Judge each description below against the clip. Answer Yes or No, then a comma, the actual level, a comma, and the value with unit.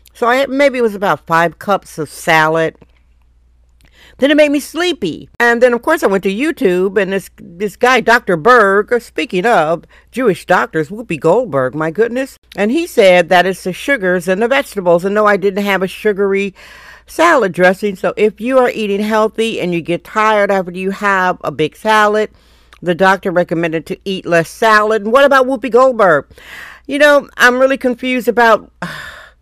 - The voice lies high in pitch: Yes, high, 205 Hz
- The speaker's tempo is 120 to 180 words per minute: No, average, 190 wpm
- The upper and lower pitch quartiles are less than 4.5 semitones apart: No, average, 5.2 semitones